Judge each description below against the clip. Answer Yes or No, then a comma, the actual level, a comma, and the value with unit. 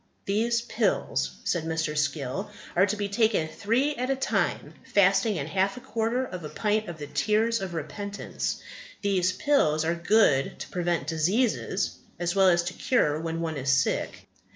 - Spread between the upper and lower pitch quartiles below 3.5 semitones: No, average, 5.2 semitones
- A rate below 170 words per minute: No, average, 175 wpm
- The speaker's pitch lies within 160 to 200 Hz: Yes, high, 190 Hz